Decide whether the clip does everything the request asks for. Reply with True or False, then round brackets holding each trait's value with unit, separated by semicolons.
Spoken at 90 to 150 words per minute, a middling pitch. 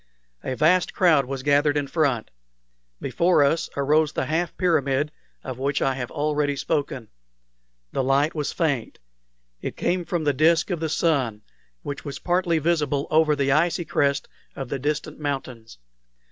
False (160 wpm; 145 Hz)